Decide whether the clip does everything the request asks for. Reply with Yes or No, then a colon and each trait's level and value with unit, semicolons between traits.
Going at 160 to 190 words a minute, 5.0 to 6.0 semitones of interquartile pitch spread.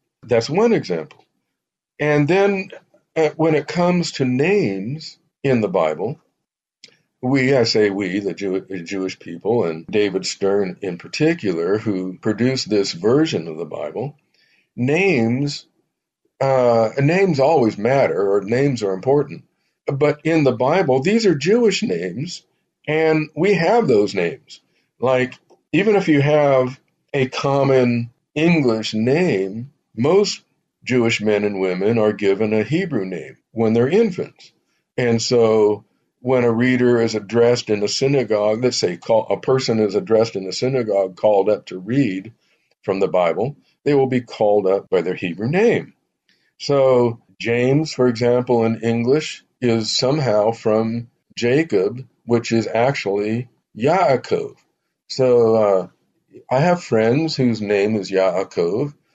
No: slow, 135 wpm; wide, 5.6 semitones